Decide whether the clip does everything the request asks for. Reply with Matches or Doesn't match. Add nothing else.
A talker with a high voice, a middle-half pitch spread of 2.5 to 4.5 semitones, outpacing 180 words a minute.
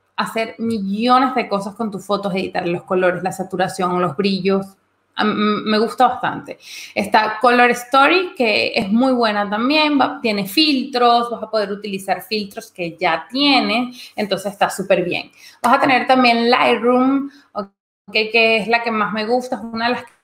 Doesn't match